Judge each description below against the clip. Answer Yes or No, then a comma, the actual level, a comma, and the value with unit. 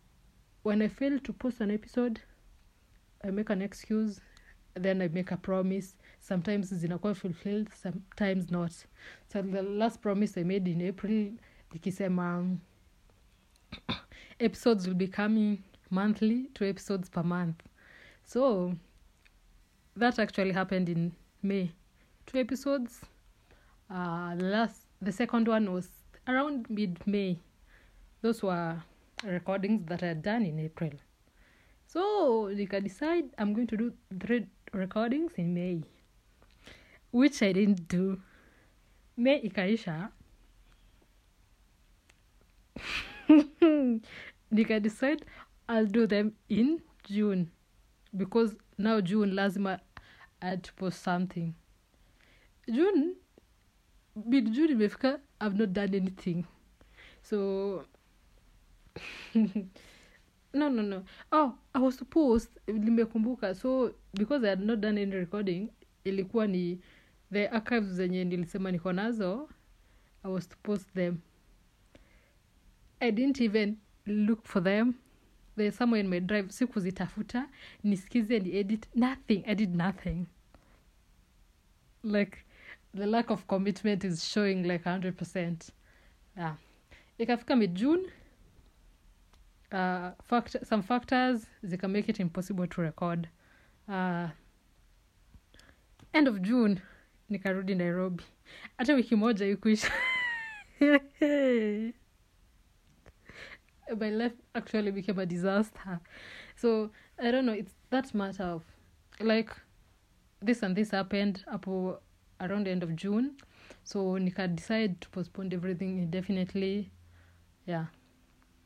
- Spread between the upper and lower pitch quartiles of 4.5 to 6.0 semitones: No, average, 3.8 semitones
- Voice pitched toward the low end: No, high, 200 Hz